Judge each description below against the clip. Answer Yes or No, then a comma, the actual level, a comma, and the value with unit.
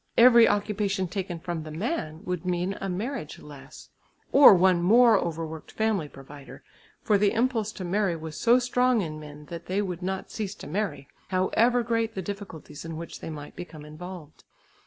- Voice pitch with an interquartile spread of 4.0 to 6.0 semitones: Yes, average, 4.9 semitones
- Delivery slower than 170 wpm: No, average, 180 wpm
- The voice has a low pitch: No, medium, 185 Hz